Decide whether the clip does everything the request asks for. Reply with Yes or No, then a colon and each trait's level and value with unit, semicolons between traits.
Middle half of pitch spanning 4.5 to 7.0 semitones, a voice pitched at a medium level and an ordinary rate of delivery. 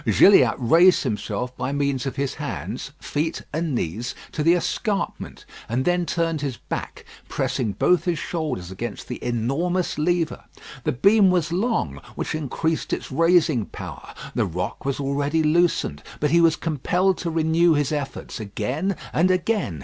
Yes: average, 5.3 semitones; medium, 155 Hz; average, 155 wpm